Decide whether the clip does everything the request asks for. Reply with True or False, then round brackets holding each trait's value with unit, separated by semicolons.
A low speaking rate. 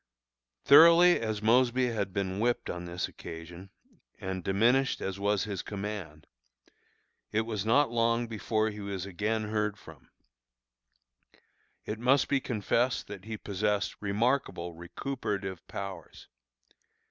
True (125 wpm)